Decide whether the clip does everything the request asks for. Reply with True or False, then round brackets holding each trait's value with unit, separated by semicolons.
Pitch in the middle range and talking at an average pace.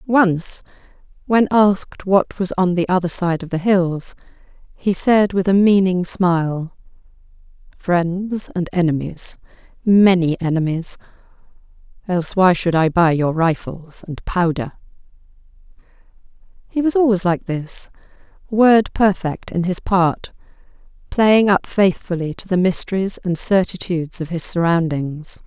False (180 Hz; 120 wpm)